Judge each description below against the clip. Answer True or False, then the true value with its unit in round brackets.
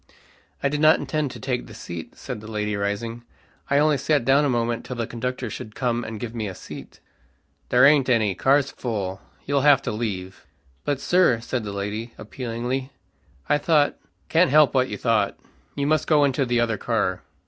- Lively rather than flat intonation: False (4.3 semitones)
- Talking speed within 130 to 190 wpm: False (200 wpm)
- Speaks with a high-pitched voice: False (120 Hz)